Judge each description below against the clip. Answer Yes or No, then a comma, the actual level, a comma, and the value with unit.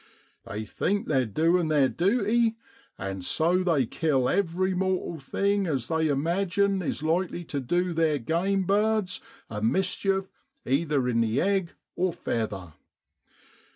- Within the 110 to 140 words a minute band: Yes, slow, 135 wpm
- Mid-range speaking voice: Yes, medium, 170 Hz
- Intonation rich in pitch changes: Yes, wide, 5.9 semitones